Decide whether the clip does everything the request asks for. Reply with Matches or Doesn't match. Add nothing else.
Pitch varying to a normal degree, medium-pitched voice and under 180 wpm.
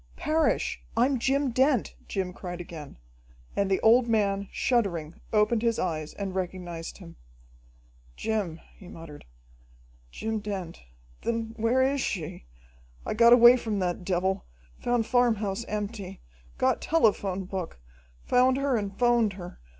Doesn't match